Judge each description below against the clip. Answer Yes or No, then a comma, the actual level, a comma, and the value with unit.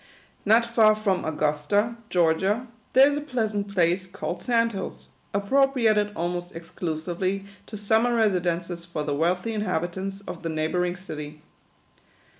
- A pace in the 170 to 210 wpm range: No, average, 140 wpm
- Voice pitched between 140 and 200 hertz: Yes, high, 190 Hz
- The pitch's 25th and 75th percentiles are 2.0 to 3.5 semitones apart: No, average, 4.2 semitones